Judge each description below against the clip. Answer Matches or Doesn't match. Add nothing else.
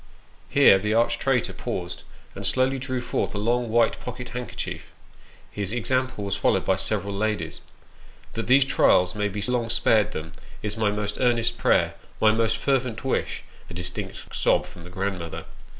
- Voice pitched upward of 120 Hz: Doesn't match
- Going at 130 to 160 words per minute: Doesn't match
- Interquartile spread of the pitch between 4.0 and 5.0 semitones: Doesn't match